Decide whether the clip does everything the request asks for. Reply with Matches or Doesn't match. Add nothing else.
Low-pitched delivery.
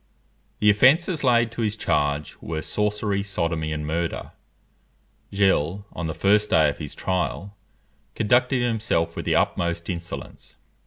Matches